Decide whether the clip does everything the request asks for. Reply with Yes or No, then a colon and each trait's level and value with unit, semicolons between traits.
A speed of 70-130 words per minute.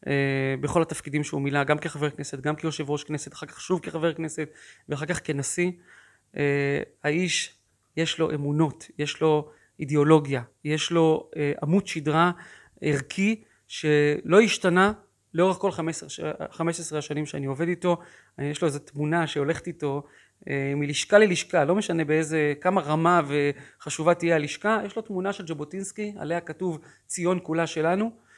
No: fast, 150 wpm